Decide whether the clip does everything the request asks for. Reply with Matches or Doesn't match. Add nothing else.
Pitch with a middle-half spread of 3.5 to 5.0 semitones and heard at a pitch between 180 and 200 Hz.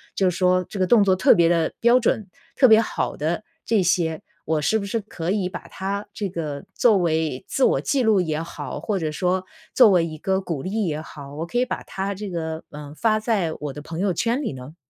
Matches